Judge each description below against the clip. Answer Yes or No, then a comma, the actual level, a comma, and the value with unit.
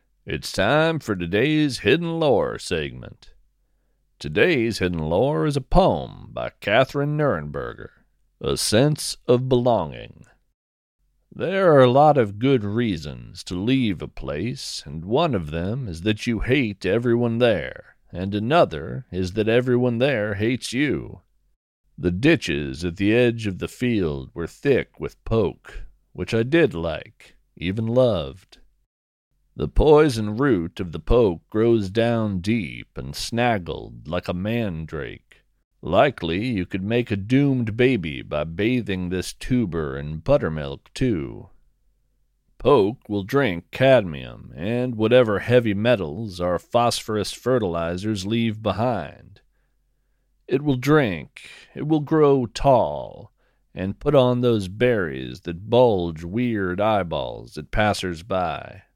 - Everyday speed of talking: No, slow, 130 wpm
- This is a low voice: Yes, low, 110 Hz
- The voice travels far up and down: Yes, wide, 5.9 semitones